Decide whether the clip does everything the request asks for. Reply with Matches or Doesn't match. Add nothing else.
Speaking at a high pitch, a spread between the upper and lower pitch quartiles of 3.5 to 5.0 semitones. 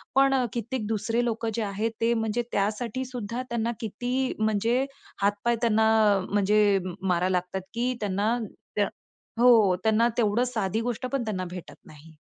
Doesn't match